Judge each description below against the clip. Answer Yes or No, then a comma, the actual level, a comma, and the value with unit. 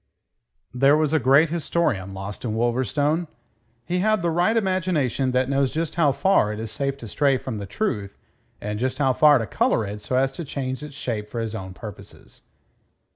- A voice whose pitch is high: No, low, 135 Hz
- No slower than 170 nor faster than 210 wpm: Yes, average, 195 wpm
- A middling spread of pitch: No, wide, 5.7 semitones